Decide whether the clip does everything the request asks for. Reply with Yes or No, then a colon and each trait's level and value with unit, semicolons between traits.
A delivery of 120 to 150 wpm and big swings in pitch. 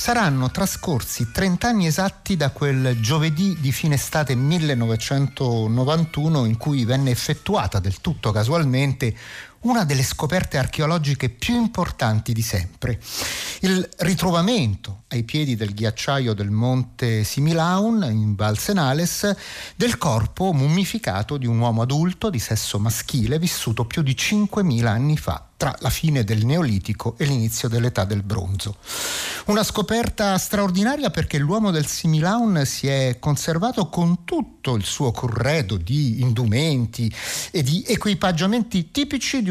Yes: average, 130 wpm; wide, 7.4 semitones